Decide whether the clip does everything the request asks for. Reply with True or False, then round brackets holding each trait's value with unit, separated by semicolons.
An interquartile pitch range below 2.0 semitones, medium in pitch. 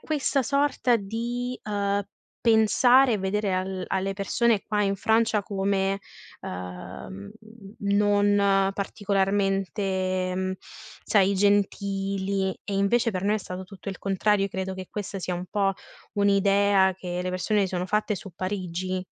False (1.6 semitones; 195 Hz)